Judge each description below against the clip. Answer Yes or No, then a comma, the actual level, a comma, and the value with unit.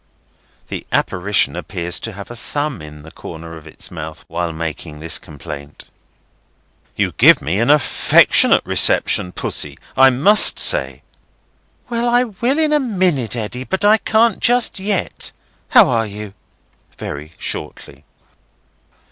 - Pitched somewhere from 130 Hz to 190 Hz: No, low, 115 Hz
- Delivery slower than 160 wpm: Yes, average, 140 wpm